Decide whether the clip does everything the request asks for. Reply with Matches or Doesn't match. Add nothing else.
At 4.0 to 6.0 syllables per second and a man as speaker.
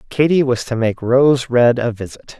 Matches